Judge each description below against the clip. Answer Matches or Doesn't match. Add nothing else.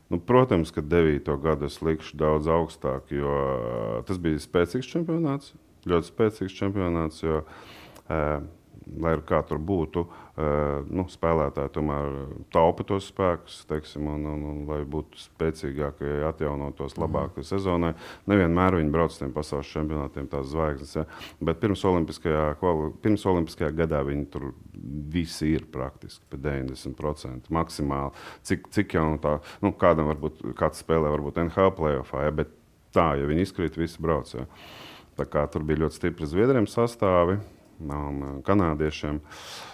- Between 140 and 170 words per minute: Matches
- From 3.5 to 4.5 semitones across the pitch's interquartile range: Doesn't match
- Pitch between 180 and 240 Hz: Doesn't match